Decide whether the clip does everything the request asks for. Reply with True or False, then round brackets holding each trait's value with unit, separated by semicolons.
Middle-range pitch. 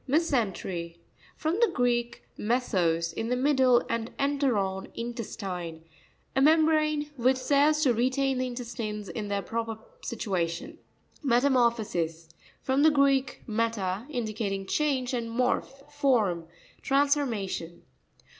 False (240 Hz)